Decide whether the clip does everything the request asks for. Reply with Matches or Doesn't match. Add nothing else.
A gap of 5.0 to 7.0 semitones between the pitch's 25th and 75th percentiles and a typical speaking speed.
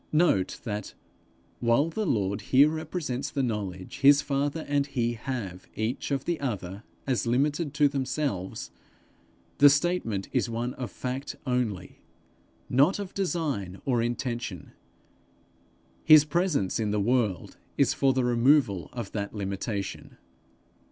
Doesn't match